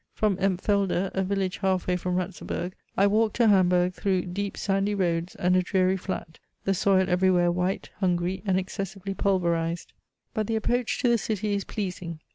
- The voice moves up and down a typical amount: No, narrow, 1.9 semitones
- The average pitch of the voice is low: No, high, 190 Hz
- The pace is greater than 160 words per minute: Yes, average, 175 wpm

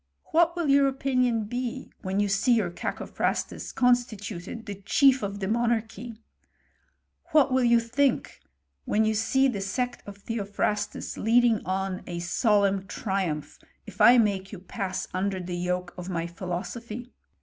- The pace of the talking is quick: No, average, 155 wpm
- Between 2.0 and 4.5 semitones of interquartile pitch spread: Yes, average, 4.1 semitones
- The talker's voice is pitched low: No, high, 210 Hz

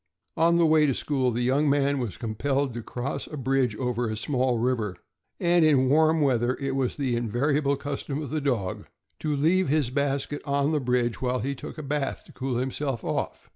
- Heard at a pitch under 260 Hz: Yes, low, 135 Hz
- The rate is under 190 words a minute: No, fast, 205 wpm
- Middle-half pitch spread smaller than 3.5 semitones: Yes, average, 2.8 semitones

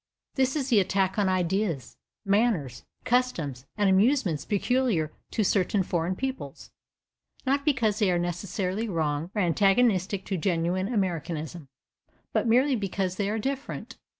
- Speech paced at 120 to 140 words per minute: Yes, slow, 135 wpm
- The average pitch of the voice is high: Yes, high, 195 Hz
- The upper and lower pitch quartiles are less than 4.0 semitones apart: No, average, 4.8 semitones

